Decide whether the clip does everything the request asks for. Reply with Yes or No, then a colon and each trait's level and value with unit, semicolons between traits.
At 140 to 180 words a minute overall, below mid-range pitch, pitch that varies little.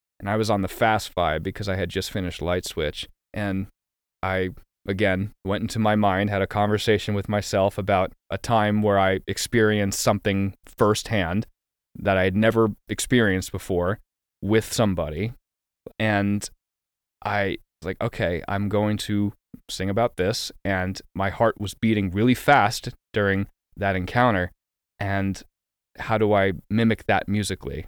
Yes: average, 150 wpm; low, 100 Hz; narrow, 2.1 semitones